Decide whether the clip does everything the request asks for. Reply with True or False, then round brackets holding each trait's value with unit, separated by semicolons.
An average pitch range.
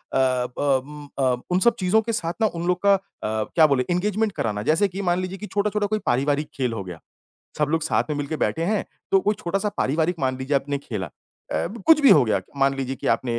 False (6.8 semitones)